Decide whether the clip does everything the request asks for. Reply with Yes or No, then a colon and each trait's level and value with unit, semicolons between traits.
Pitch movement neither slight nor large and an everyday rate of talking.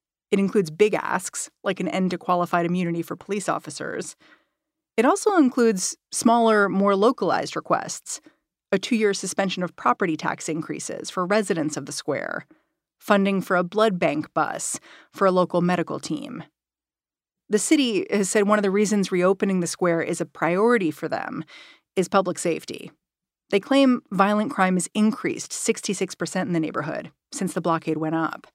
Yes: average, 3.6 semitones; average, 165 wpm